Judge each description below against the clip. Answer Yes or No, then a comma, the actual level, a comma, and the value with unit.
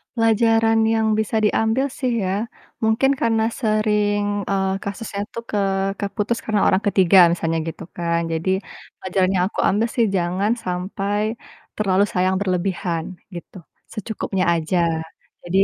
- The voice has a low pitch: No, high, 200 Hz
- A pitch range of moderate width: Yes, average, 3.1 semitones